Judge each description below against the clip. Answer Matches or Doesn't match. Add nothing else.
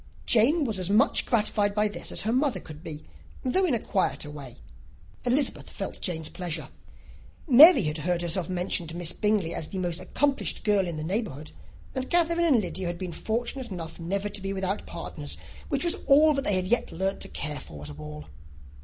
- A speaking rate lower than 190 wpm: Doesn't match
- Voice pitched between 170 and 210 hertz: Matches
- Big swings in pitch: Matches